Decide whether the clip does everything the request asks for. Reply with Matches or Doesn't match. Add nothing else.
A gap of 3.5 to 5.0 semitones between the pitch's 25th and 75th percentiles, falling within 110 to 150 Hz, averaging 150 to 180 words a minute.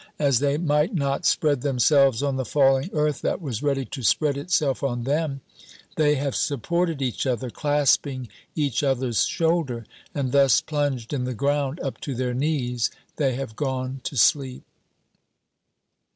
Doesn't match